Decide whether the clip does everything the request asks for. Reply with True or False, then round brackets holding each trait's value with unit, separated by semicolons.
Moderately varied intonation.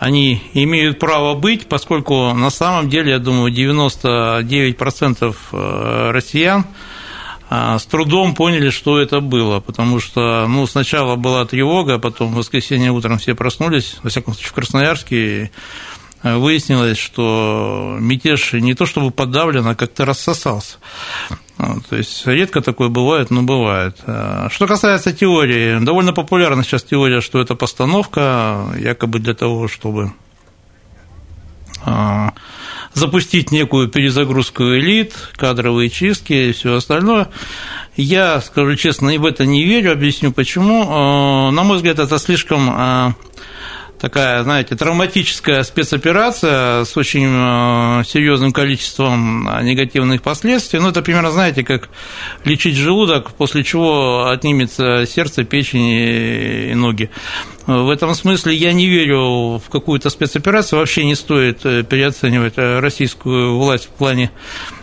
True (4.1 semitones)